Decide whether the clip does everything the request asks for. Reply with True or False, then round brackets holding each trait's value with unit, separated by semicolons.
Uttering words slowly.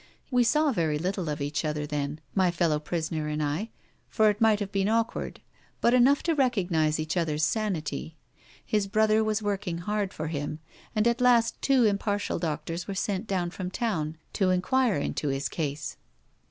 False (180 wpm)